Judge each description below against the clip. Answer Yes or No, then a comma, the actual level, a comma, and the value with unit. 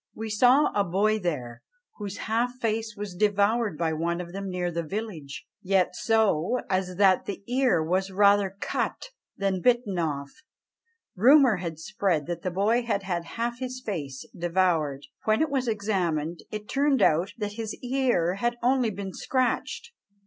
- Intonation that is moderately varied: Yes, average, 4.7 semitones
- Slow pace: No, average, 165 wpm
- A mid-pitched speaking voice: No, high, 200 Hz